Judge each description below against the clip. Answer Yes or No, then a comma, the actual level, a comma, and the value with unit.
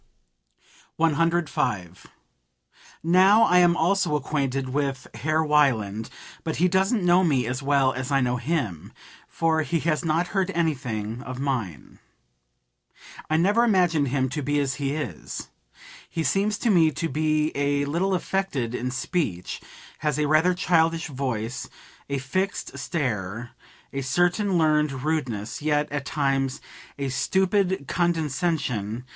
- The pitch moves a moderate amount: Yes, average, 4.7 semitones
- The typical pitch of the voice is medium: Yes, medium, 150 Hz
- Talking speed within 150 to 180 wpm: No, slow, 135 wpm